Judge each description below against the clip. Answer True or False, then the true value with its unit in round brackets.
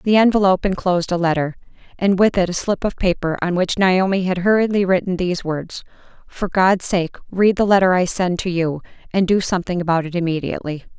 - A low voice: False (185 Hz)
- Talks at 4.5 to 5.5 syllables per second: False (5.9 syllables/s)